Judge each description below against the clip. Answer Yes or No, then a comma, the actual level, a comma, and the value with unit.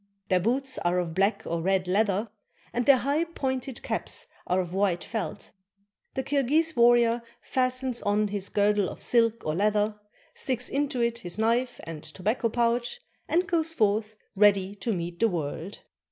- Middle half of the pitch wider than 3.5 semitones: Yes, average, 4.7 semitones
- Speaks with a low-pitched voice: No, high, 220 Hz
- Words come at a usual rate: Yes, average, 170 wpm